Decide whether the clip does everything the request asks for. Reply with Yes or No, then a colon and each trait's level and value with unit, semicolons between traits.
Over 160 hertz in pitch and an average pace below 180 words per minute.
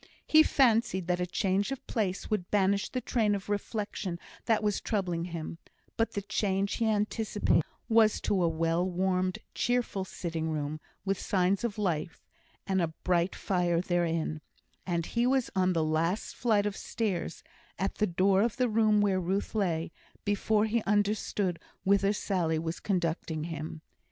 Yes: high, 190 Hz; average, 160 wpm